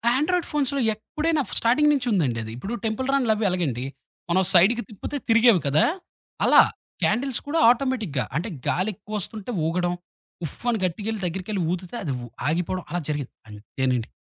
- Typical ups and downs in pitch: No, wide, 6.4 semitones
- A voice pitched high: Yes, high, 210 Hz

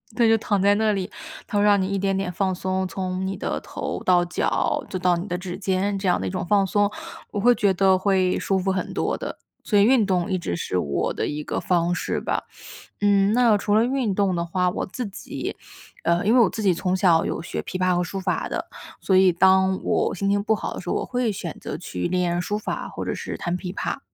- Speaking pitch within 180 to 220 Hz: Yes, high, 190 Hz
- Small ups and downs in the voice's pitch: Yes, narrow, 2.2 semitones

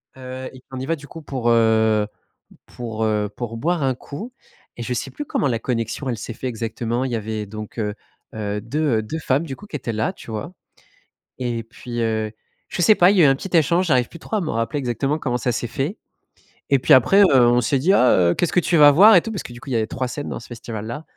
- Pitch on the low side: Yes, low, 125 Hz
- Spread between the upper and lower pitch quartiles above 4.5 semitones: Yes, average, 5.0 semitones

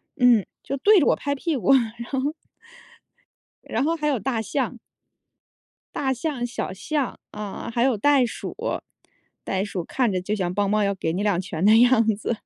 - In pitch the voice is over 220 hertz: Yes, high, 235 Hz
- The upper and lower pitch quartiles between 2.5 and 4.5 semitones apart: No, average, 4.9 semitones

